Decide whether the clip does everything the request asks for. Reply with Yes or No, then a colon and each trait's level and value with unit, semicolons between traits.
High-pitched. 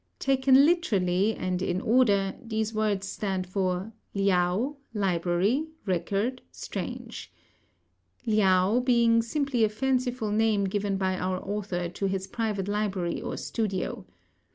Yes: high, 205 Hz